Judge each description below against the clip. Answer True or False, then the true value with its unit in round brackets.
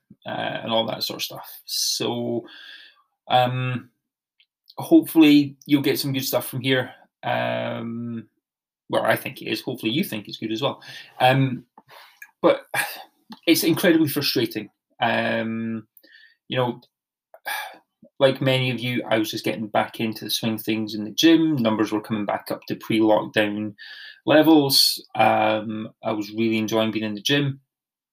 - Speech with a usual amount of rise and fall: True (4.2 semitones)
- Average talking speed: True (155 wpm)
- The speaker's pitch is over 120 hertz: False (115 Hz)